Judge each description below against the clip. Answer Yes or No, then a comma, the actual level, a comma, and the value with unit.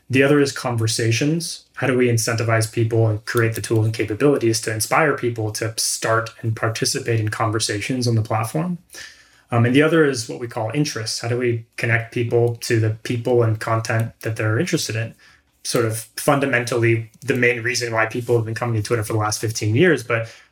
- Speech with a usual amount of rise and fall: No, narrow, 1.8 semitones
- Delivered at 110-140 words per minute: No, average, 200 wpm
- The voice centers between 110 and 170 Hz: Yes, low, 115 Hz